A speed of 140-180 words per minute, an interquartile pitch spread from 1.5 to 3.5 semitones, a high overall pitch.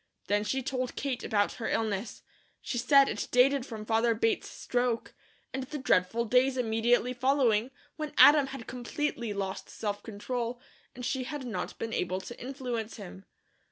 Yes: average, 160 wpm; average, 2.9 semitones; high, 240 Hz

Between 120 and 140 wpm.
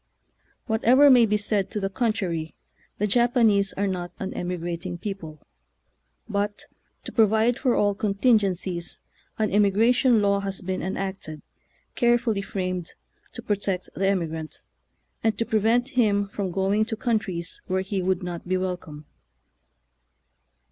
Yes: slow, 135 wpm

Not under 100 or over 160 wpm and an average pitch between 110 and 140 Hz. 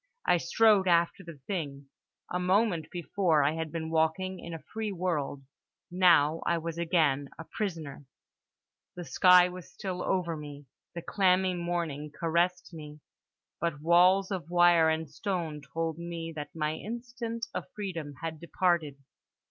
No: average, 150 wpm; medium, 170 Hz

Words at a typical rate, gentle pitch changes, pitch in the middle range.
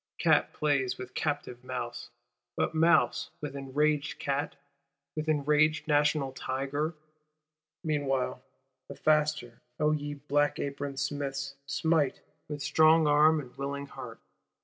No: slow, 120 wpm; narrow, 1.8 semitones; medium, 145 Hz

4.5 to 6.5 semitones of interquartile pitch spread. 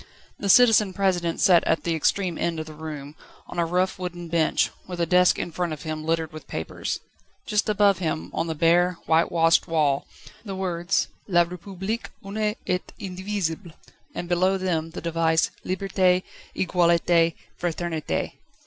No: narrow, 2.4 semitones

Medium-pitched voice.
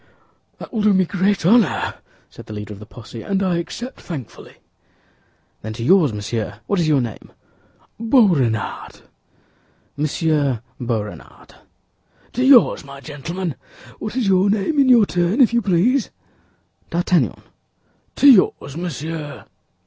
Yes: medium, 170 Hz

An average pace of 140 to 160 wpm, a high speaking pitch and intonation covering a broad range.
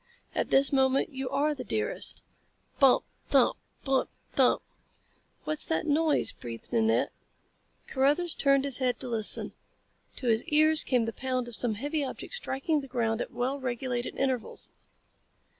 No: average, 155 wpm; very high, 265 Hz; average, 2.9 semitones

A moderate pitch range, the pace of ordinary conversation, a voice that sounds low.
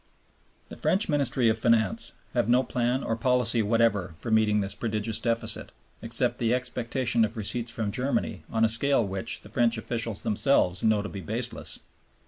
No: narrow, 2.3 semitones; average, 170 wpm; low, 115 Hz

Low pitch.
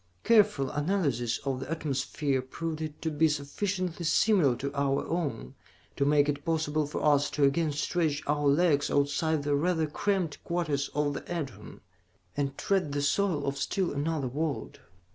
No: medium, 150 Hz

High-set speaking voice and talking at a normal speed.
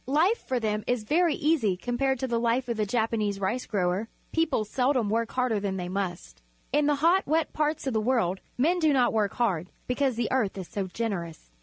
No: high, 235 Hz; fast, 210 wpm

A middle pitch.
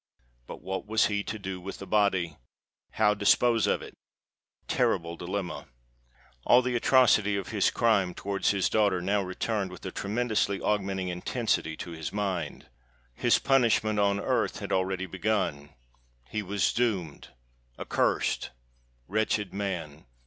No: low, 100 Hz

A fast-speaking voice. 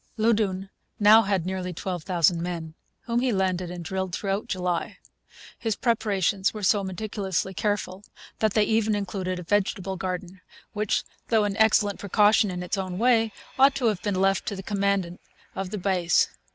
No: average, 165 wpm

